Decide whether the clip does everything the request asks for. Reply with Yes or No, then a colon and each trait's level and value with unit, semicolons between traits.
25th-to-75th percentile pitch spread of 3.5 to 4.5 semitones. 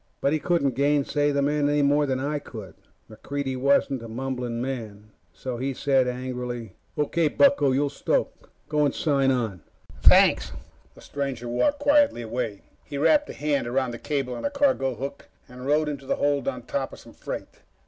No: average, 2.8 semitones